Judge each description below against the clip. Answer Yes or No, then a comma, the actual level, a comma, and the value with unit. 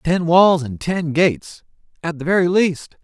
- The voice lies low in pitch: No, medium, 165 Hz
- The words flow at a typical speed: Yes, average, 160 wpm